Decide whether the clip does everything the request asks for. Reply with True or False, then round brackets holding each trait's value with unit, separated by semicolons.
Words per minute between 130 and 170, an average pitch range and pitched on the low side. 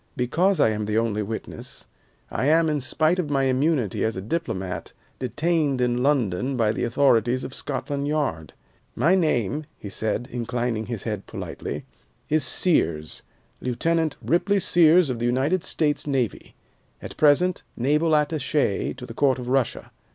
True (155 wpm; 5.0 semitones; 130 Hz)